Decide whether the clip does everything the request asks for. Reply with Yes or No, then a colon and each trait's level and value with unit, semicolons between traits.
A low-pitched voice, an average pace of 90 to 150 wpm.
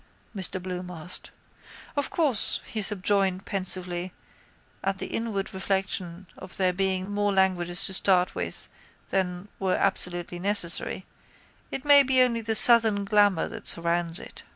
No: high, 190 Hz; average, 140 wpm